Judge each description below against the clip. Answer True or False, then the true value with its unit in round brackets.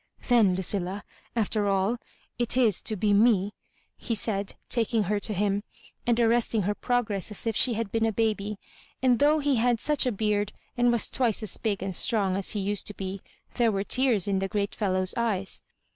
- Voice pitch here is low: False (210 Hz)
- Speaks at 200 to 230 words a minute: True (205 wpm)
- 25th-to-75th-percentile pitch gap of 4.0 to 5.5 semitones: False (2.9 semitones)